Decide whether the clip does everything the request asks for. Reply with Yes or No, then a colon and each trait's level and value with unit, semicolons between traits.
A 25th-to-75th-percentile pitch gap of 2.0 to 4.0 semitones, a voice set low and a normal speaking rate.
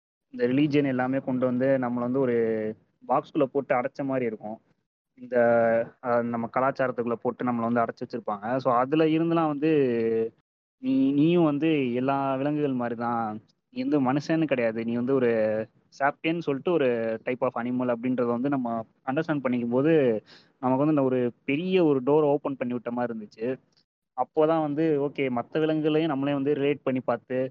No: average, 3.6 semitones; low, 130 Hz; fast, 160 wpm